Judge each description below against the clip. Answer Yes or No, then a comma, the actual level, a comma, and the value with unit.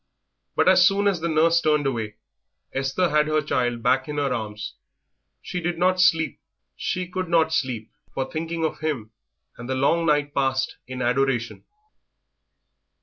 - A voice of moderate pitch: Yes, medium, 150 Hz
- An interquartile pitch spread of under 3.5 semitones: No, average, 4.5 semitones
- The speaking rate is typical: Yes, average, 160 wpm